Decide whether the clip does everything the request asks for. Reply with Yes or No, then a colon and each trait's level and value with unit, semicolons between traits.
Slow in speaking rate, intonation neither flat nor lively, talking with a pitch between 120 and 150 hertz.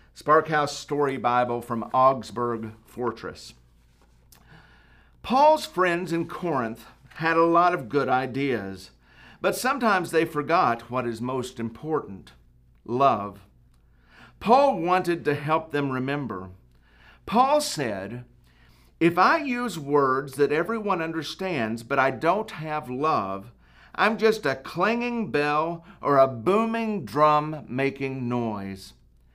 No: slow, 115 wpm; wide, 6.8 semitones; medium, 140 Hz